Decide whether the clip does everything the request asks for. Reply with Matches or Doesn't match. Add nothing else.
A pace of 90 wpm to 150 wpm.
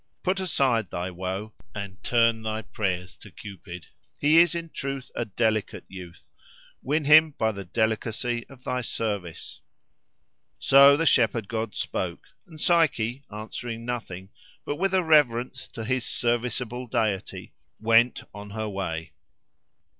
Matches